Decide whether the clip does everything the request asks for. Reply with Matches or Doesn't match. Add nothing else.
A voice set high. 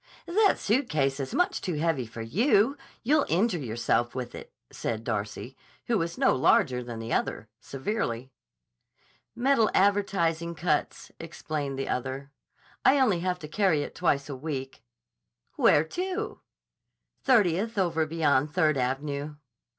Doesn't match